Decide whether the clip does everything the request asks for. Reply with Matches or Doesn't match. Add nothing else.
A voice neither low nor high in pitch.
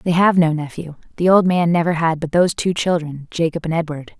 Matches